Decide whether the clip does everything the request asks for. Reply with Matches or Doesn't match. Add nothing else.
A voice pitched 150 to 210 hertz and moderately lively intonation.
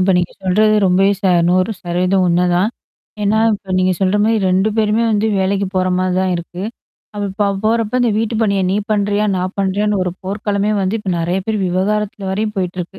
Doesn't match